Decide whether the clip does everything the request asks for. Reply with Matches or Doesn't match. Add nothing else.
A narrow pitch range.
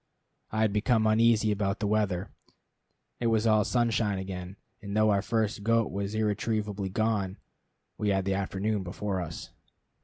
Matches